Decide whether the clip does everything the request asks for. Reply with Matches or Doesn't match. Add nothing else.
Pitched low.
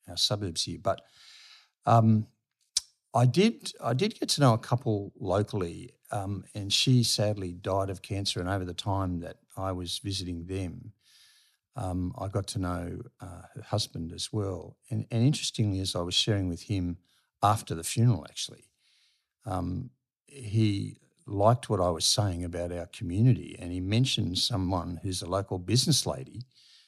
Matches